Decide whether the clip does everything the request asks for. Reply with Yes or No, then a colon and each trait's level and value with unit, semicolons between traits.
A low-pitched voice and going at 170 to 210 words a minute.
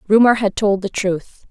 No: high, 205 Hz; average, 200 wpm